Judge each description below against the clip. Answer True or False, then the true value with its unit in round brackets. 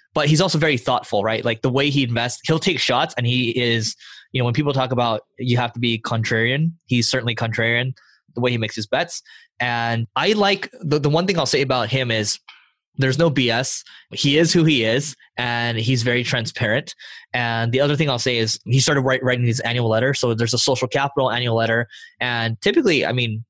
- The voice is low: True (125 Hz)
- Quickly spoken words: True (220 wpm)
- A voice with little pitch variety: False (3.1 semitones)